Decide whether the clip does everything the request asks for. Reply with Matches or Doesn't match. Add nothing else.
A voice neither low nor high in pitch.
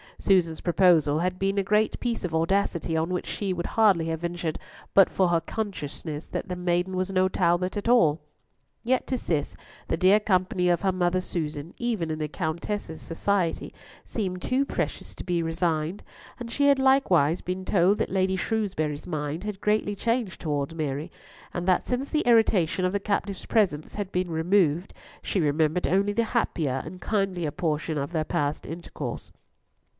Matches